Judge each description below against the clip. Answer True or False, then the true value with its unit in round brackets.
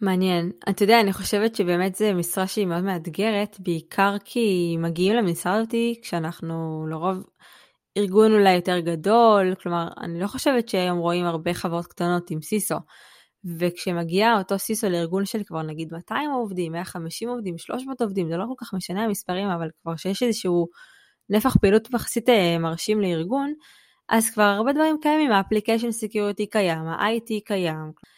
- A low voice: False (195 Hz)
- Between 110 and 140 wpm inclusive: False (150 wpm)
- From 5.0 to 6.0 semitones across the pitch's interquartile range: False (4.1 semitones)